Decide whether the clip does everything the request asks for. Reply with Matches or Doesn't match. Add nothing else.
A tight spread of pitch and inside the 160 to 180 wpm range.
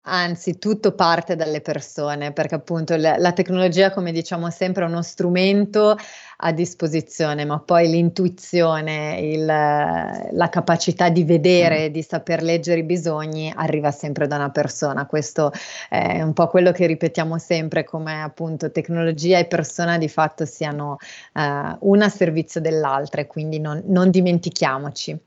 Doesn't match